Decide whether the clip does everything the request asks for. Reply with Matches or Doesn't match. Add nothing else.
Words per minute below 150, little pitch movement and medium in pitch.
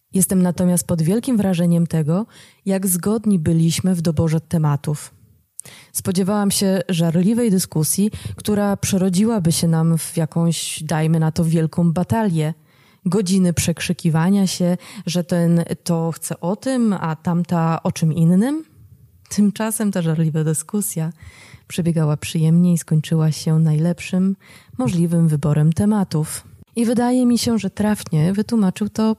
Doesn't match